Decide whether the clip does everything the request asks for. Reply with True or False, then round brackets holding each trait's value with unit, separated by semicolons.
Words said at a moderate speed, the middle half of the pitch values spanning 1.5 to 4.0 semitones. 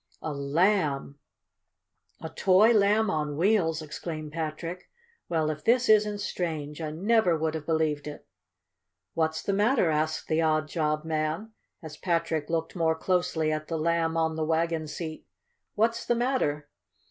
True (150 wpm; 3.1 semitones)